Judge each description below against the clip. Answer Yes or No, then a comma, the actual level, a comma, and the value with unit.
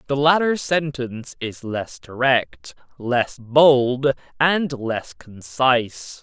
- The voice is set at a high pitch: No, low, 130 Hz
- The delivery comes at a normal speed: No, slow, 105 wpm